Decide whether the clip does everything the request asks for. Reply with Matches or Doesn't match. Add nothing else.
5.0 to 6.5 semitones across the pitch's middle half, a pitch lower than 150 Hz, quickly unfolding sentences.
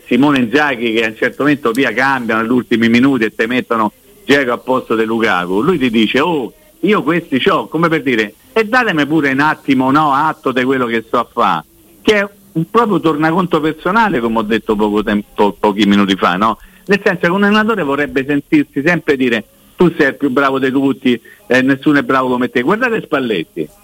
Matches